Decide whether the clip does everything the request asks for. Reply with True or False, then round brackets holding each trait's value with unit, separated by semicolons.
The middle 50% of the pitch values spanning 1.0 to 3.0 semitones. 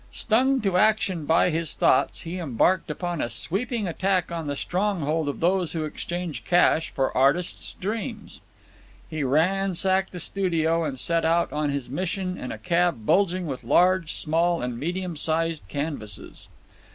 False (3.4 semitones)